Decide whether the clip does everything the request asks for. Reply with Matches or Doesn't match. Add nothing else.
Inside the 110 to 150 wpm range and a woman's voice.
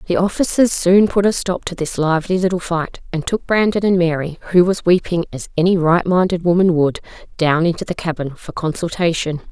Doesn't match